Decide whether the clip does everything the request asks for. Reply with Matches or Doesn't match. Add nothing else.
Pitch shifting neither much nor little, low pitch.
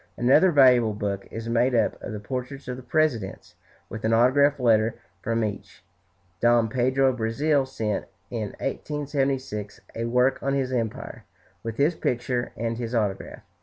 Matches